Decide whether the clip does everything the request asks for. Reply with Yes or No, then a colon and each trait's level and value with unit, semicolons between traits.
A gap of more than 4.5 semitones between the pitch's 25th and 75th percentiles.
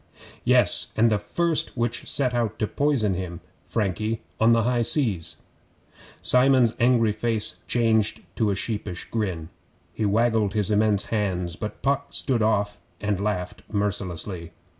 No: narrow, 2.6 semitones